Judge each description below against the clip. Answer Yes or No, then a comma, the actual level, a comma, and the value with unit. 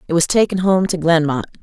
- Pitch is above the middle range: No, medium, 170 Hz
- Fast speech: Yes, fast, 220 wpm